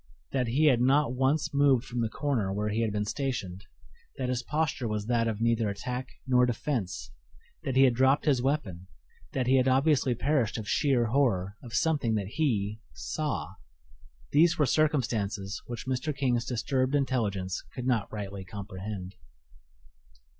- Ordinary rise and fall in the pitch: Yes, average, 4.3 semitones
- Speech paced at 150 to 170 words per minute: Yes, average, 160 wpm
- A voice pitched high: No, low, 125 Hz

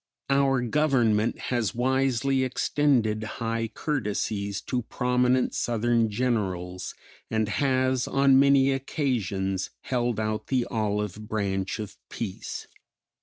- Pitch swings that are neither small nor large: Yes, average, 3.7 semitones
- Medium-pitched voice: No, low, 120 Hz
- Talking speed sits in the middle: No, slow, 105 wpm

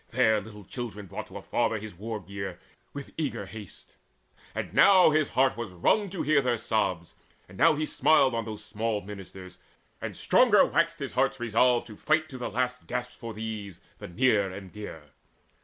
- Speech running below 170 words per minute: No, average, 190 wpm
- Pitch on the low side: Yes, low, 115 Hz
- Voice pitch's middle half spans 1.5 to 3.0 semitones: No, average, 4.5 semitones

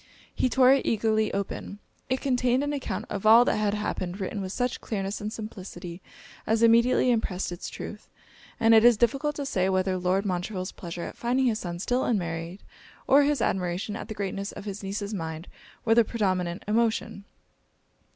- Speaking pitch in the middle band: No, high, 210 Hz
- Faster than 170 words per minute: Yes, average, 180 wpm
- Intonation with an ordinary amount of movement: Yes, average, 4.1 semitones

